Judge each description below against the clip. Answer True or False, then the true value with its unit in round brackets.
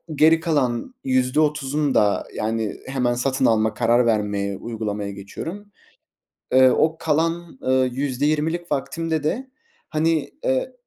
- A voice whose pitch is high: False (130 Hz)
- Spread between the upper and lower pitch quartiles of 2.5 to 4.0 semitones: False (5.3 semitones)